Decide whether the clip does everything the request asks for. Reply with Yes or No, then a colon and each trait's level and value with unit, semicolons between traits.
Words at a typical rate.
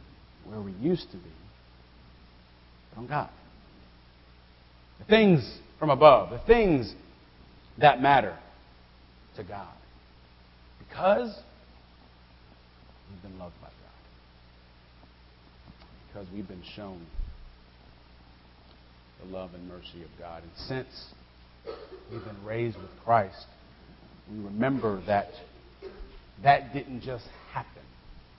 No: slow, 100 wpm